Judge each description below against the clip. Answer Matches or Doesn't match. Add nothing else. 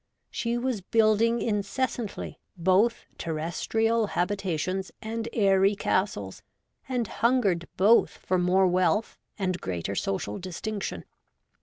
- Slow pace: Matches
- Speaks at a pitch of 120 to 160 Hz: Doesn't match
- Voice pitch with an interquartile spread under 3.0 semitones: Doesn't match